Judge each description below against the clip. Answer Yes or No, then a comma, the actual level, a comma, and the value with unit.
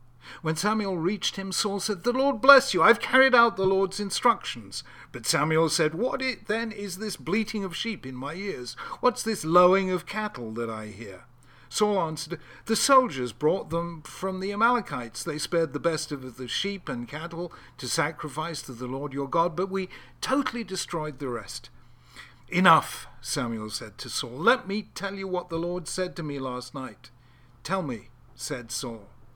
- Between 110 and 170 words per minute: No, average, 185 wpm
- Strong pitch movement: Yes, wide, 7.6 semitones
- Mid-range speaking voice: Yes, medium, 170 Hz